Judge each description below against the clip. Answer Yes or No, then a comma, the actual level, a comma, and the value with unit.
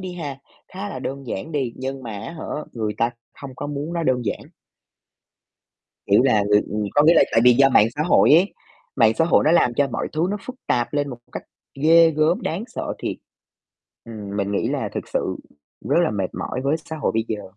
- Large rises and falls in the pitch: Yes, wide, 5.7 semitones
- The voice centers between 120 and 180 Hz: Yes, low, 135 Hz